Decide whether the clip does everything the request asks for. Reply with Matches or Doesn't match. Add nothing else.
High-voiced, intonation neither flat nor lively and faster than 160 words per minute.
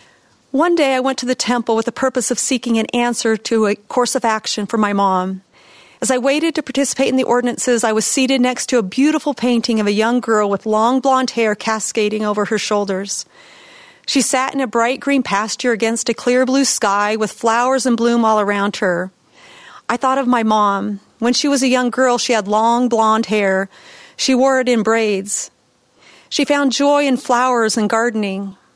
Matches